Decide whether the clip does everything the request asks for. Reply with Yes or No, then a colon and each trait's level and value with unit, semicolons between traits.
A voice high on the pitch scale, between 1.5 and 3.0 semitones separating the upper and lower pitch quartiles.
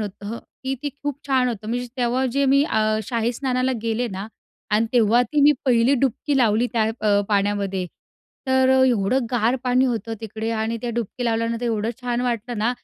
Yes: high, 235 Hz; average, 2.7 semitones